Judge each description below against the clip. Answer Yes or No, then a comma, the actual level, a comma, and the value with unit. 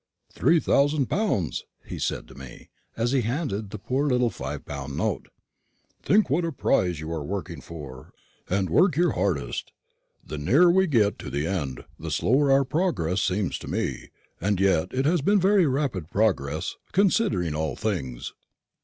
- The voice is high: No, low, 105 Hz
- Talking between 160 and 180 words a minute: Yes, average, 170 wpm